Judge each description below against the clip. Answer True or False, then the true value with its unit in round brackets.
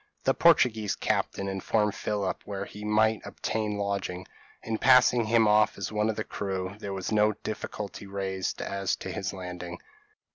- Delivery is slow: False (160 wpm)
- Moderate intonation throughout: False (1.8 semitones)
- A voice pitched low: True (105 Hz)